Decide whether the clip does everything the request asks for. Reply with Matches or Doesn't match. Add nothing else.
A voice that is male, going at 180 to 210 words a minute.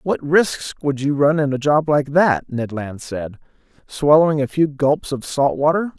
Matches